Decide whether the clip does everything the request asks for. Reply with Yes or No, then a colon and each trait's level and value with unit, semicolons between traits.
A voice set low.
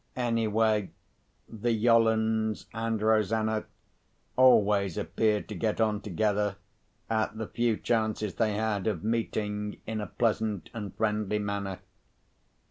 Yes: low, 110 Hz